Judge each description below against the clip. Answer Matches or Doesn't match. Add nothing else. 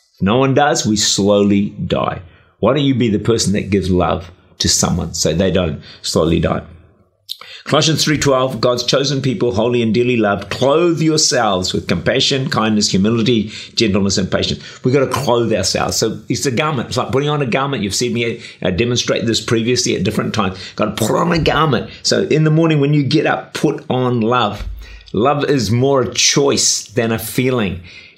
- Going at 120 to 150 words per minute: Doesn't match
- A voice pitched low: Matches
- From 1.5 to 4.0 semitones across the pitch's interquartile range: Doesn't match